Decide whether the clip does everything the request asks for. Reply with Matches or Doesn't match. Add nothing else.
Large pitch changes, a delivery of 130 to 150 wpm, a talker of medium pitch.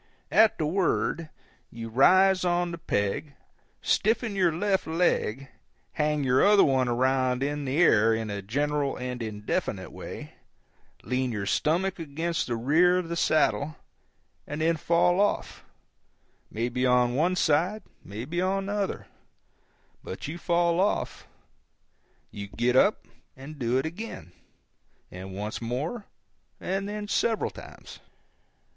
Matches